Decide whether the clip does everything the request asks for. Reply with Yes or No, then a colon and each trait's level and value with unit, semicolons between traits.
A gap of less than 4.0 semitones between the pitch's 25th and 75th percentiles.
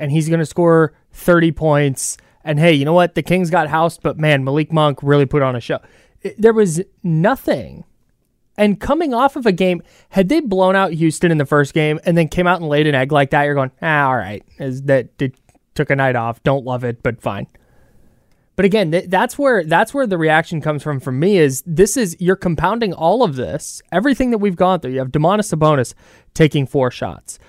No: average, 4.5 semitones